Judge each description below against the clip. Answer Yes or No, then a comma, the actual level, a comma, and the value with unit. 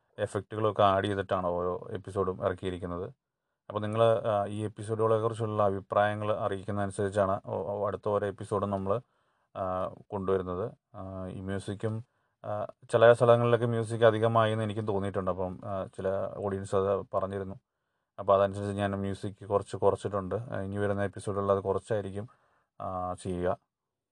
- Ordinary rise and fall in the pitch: No, narrow, 2.0 semitones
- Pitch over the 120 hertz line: No, low, 100 Hz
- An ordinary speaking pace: Yes, average, 110 wpm